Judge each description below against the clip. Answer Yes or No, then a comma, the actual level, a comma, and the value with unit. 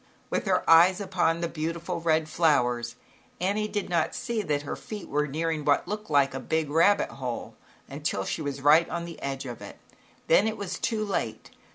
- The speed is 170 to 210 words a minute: Yes, average, 195 wpm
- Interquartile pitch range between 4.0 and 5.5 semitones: Yes, average, 4.3 semitones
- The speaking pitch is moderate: Yes, medium, 165 Hz